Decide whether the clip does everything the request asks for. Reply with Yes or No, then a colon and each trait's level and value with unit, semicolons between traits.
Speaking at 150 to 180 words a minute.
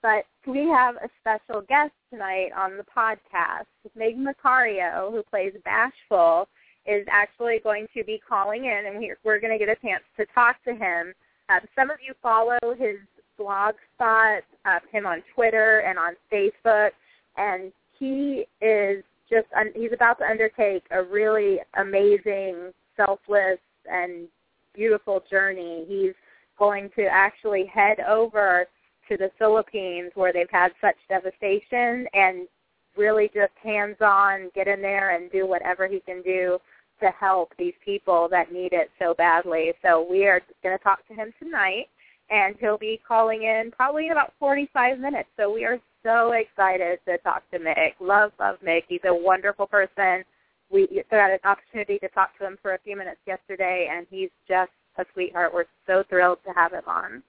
Yes: average, 170 wpm